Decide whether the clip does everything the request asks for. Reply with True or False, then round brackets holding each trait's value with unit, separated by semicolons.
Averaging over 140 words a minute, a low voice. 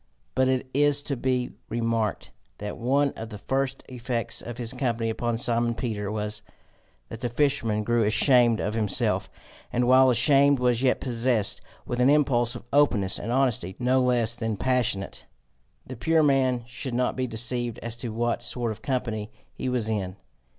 True (170 wpm; 120 Hz)